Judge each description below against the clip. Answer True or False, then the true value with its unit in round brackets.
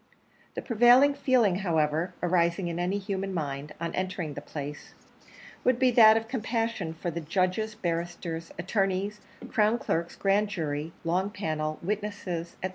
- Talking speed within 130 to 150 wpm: True (145 wpm)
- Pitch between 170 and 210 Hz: True (185 Hz)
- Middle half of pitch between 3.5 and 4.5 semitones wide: True (4.1 semitones)